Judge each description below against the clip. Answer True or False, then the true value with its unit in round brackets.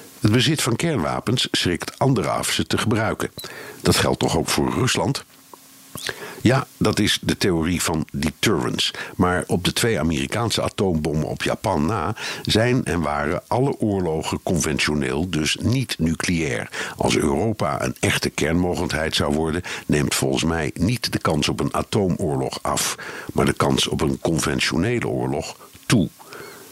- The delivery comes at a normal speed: True (150 wpm)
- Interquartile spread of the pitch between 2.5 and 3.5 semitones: False (4.1 semitones)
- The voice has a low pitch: True (80 Hz)